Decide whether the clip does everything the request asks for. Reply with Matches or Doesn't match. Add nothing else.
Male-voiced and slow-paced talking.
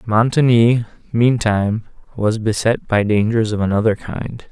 Matches